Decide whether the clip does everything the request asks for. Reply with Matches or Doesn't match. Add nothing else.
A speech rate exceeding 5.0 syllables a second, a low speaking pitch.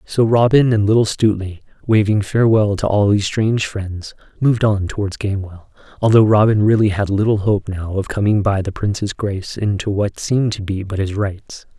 Matches